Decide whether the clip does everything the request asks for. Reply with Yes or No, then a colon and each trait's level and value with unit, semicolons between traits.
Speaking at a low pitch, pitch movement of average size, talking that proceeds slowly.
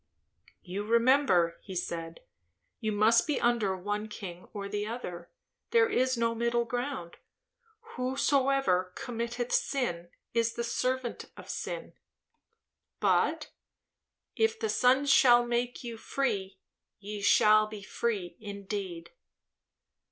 No: high, 230 Hz; average, 4.1 semitones; slow, 115 wpm